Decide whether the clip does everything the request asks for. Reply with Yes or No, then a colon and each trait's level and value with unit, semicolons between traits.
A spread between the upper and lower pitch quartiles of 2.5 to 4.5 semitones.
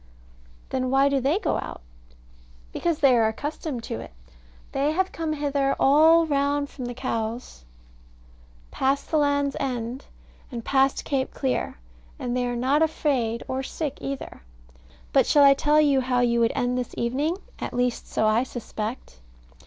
Yes: average, 2.9 semitones